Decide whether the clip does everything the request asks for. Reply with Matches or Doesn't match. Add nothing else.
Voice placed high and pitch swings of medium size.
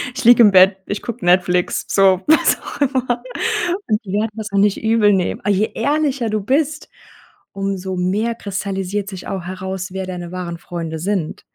Matches